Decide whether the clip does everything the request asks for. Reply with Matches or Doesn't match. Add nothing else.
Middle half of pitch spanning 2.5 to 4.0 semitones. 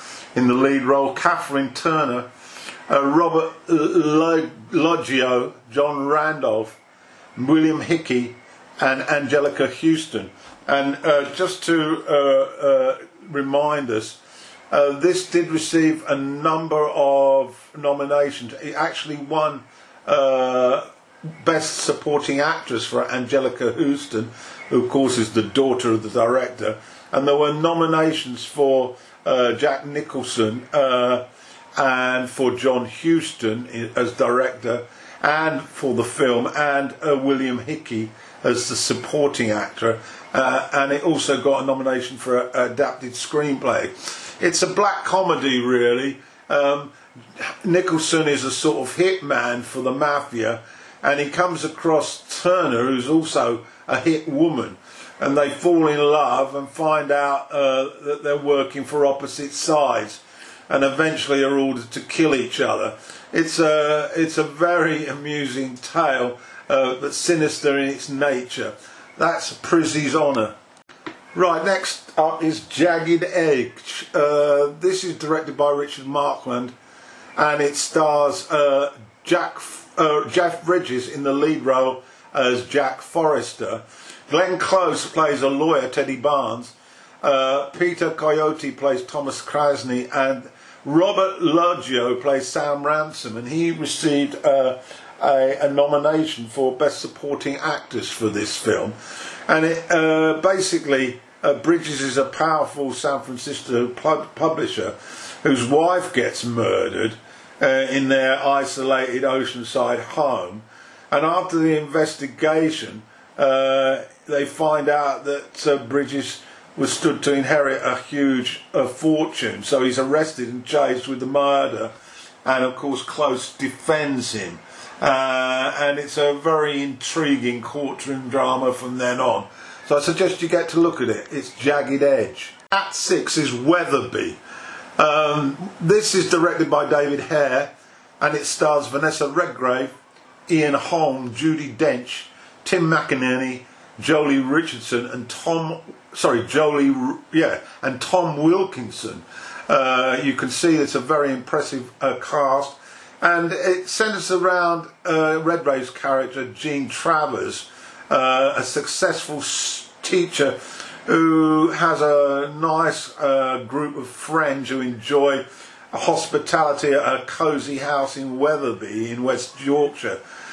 Matches